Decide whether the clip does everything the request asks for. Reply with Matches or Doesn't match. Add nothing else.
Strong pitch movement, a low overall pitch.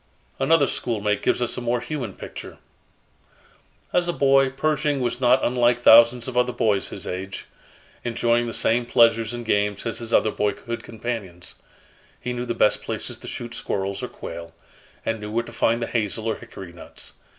Doesn't match